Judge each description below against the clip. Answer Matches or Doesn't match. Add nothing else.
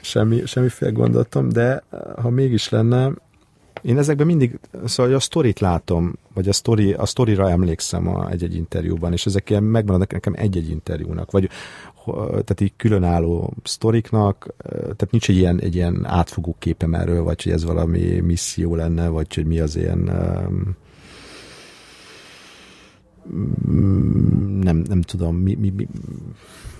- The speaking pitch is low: Matches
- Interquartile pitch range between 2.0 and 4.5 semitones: Doesn't match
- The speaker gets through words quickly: Doesn't match